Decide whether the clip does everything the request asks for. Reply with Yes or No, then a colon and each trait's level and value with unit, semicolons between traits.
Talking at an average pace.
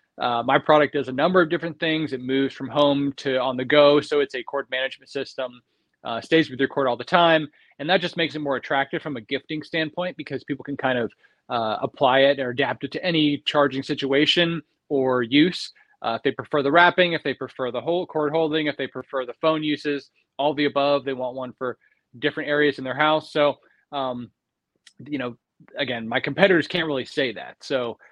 No: fast, 220 wpm